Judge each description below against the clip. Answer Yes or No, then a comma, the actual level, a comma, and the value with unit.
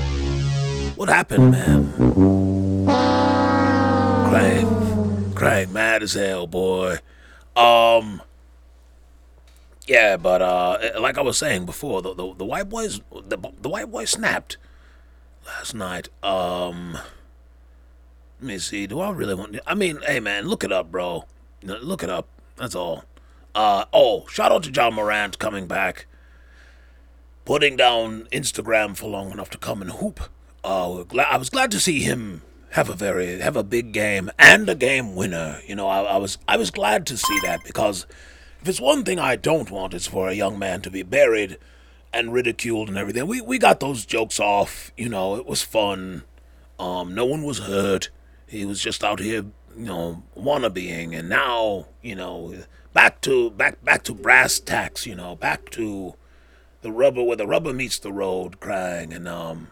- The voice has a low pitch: Yes, very low, 90 Hz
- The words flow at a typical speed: Yes, average, 170 wpm